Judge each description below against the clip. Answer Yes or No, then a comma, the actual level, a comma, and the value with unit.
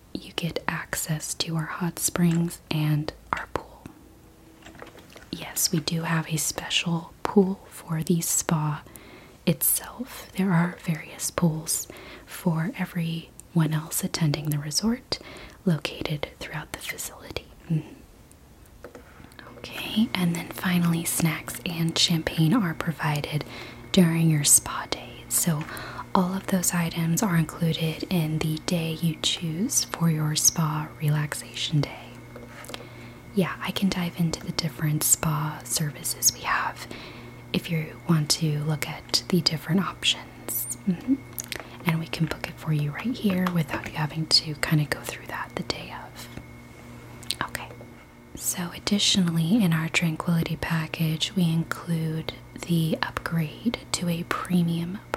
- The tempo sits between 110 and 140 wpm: Yes, slow, 135 wpm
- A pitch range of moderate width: No, narrow, 2.2 semitones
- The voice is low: No, medium, 165 Hz